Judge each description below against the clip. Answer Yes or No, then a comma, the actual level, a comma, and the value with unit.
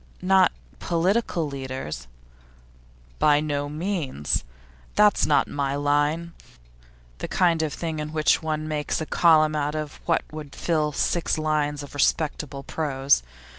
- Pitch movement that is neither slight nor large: No, narrow, 2.1 semitones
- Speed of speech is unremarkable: No, slow, 130 wpm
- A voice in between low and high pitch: Yes, medium, 155 Hz